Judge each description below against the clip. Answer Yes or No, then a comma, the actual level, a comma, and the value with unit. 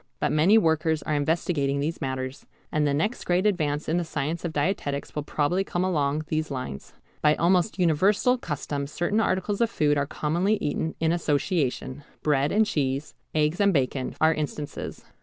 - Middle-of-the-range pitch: Yes, medium, 155 Hz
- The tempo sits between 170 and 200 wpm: Yes, average, 175 wpm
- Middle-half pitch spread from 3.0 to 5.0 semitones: Yes, average, 3.6 semitones